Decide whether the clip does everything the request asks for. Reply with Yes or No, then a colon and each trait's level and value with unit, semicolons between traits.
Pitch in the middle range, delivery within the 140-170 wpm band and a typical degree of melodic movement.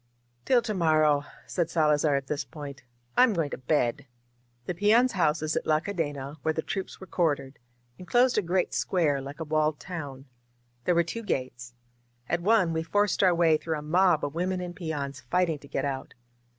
No: medium, 160 Hz; average, 190 wpm; average, 3.9 semitones